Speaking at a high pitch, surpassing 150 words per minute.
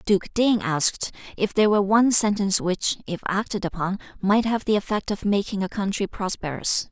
Yes: high, 200 Hz; average, 180 wpm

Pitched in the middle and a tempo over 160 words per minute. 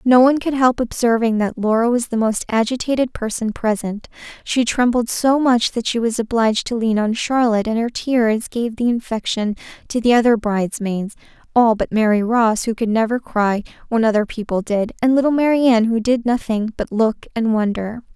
No: high, 230 Hz; average, 185 wpm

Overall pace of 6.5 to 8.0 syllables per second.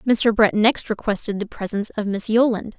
No: 5.4 syllables/s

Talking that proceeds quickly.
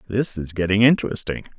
No: average, 150 wpm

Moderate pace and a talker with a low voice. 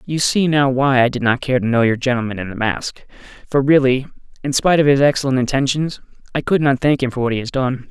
No: fast, 250 wpm; low, 130 Hz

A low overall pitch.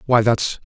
Yes: low, 115 Hz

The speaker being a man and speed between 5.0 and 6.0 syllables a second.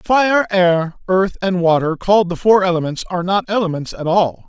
Yes: male; 5.1 syllables/s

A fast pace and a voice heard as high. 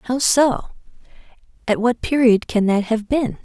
No: average, 140 wpm; high, 240 Hz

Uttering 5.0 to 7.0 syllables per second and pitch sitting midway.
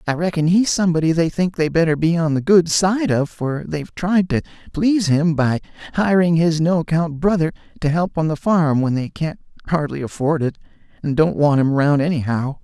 Yes: 5.4 syllables/s; medium, 160 Hz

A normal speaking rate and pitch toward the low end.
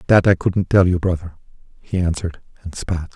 Yes: average, 190 wpm; very low, 90 Hz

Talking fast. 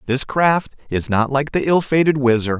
Yes: fast, 210 wpm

